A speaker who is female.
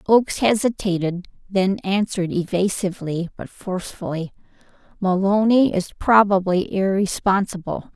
Yes: female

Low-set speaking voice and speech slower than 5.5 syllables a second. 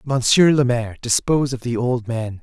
Yes: low, 125 Hz; 5.2 syllables/s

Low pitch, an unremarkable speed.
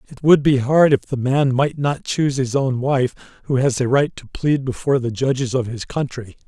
No: low, 130 Hz; fast, 230 wpm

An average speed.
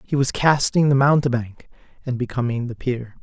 Yes: average, 165 wpm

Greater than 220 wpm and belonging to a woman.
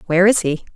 Yes: fast, 240 wpm; female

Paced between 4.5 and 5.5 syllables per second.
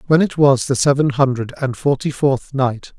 Yes: 4.7 syllables/s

